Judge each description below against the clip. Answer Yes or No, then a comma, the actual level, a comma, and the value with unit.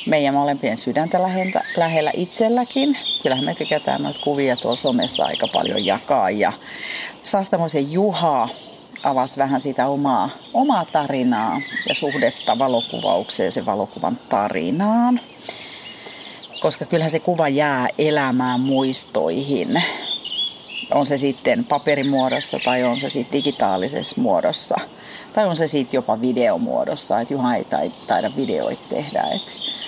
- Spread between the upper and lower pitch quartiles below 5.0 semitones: No, average, 5.3 semitones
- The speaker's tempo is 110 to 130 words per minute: Yes, average, 120 wpm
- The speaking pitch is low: No, medium, 145 Hz